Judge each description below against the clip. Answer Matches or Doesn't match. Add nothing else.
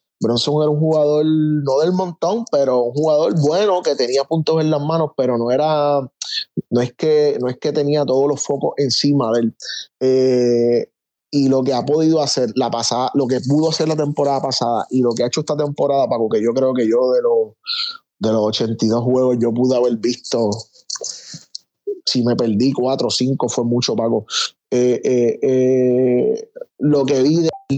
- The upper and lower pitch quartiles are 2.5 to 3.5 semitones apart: Doesn't match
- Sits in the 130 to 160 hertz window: Matches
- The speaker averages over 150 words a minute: Matches